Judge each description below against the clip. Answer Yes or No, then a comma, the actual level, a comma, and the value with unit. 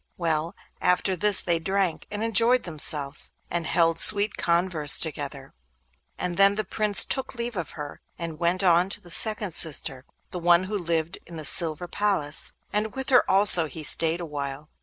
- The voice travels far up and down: No, average, 4.1 semitones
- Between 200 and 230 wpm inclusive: No, average, 175 wpm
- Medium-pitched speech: Yes, medium, 175 Hz